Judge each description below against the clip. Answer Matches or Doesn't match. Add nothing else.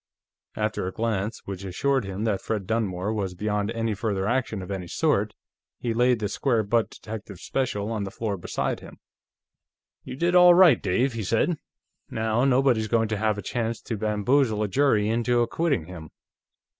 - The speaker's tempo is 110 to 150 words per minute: Doesn't match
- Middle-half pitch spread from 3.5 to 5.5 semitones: Doesn't match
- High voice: Doesn't match